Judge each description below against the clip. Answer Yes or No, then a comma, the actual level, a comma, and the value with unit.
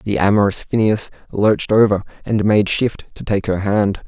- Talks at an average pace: Yes, average, 175 wpm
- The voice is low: Yes, low, 105 Hz